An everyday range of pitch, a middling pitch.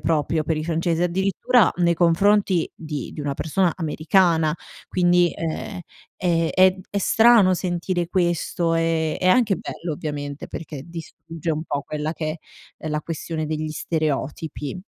No: narrow, 2.3 semitones; medium, 165 Hz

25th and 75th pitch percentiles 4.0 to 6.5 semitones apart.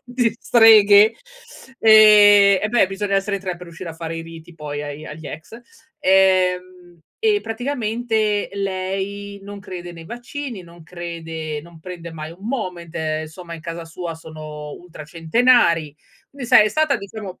Yes: average, 4.4 semitones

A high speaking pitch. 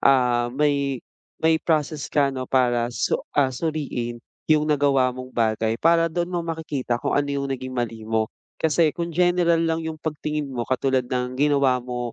No: medium, 140 Hz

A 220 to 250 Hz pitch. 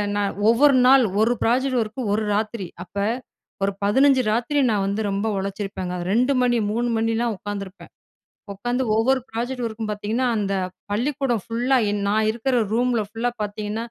Yes: high, 225 Hz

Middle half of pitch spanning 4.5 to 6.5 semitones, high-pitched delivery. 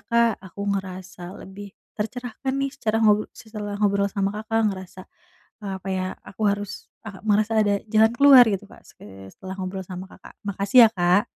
No: narrow, 2.6 semitones; high, 205 Hz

